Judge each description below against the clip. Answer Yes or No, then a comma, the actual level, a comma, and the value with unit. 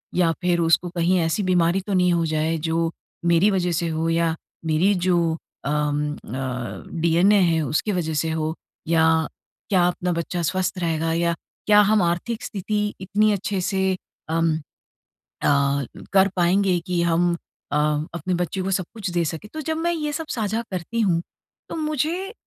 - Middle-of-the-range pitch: Yes, medium, 175 Hz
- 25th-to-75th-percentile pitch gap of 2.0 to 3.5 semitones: Yes, average, 2.9 semitones